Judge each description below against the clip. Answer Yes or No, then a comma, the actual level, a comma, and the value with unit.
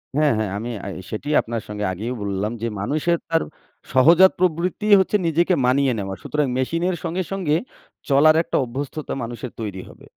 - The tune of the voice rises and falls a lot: Yes, wide, 6.5 semitones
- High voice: No, medium, 140 Hz